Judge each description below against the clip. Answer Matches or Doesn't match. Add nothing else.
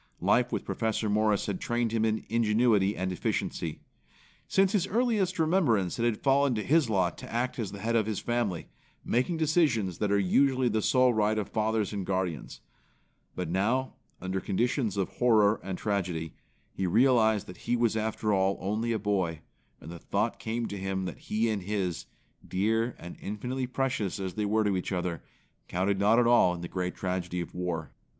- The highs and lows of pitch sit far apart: Doesn't match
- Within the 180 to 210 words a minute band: Matches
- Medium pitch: Doesn't match